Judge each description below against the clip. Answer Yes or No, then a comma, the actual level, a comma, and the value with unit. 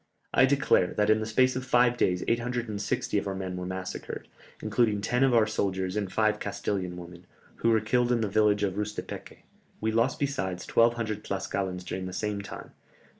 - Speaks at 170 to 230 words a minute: Yes, average, 185 wpm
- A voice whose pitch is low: Yes, low, 105 Hz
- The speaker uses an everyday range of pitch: Yes, average, 3.6 semitones